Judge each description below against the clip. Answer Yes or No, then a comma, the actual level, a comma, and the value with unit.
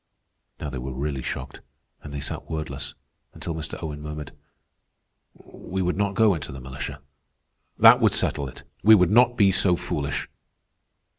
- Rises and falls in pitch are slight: No, average, 5.2 semitones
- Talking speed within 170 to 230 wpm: No, average, 160 wpm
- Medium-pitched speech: No, very low, 75 Hz